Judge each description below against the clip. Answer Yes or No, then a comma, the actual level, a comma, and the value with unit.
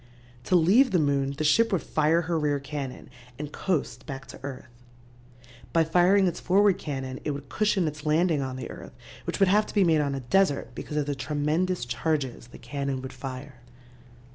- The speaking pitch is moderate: Yes, medium, 150 Hz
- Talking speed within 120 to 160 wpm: No, average, 195 wpm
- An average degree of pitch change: Yes, average, 4.4 semitones